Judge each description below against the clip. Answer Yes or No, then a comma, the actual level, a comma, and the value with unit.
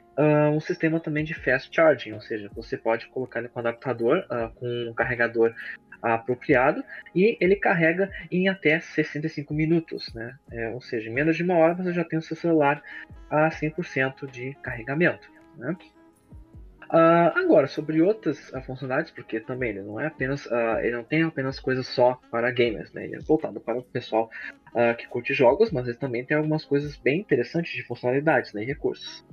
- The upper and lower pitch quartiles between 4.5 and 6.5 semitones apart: Yes, average, 5.1 semitones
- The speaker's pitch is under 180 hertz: Yes, medium, 140 Hz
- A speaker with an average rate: No, fast, 190 wpm